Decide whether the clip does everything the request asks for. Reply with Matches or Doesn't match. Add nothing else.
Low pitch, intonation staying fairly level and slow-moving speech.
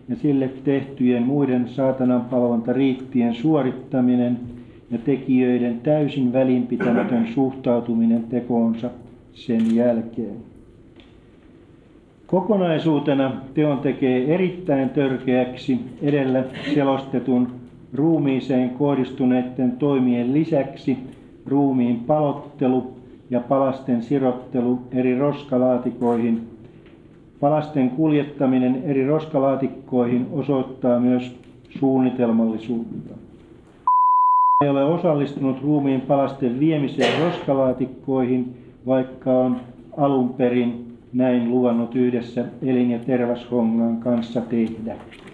Matches